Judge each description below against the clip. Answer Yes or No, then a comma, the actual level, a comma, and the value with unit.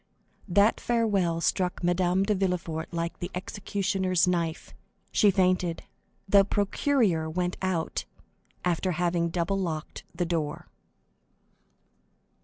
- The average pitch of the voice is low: No, medium, 180 Hz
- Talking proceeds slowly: Yes, slow, 105 wpm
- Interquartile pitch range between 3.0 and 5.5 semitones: No, narrow, 2.4 semitones